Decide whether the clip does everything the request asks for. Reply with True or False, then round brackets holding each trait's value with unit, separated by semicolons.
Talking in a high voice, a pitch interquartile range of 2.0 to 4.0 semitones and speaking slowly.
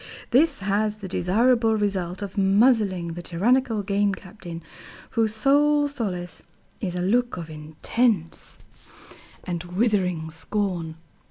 False (200 Hz; 4.4 semitones; 115 wpm)